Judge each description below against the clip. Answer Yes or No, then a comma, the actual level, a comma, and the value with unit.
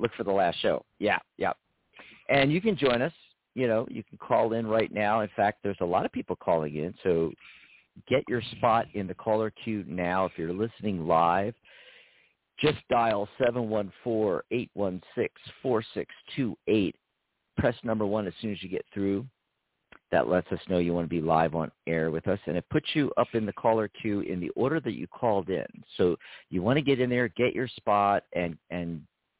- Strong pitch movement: No, average, 4.6 semitones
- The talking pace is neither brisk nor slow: No, fast, 210 wpm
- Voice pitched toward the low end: Yes, low, 105 Hz